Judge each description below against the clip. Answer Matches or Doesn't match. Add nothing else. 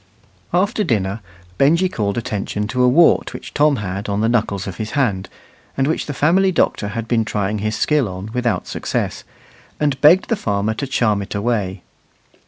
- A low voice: Matches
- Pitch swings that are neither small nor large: Doesn't match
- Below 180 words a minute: Doesn't match